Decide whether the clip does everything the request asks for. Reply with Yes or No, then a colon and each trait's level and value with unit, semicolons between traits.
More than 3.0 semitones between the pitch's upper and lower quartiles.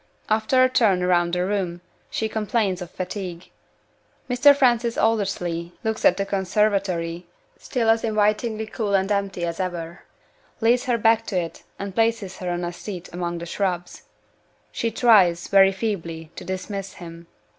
Yes: average, 4.0 semitones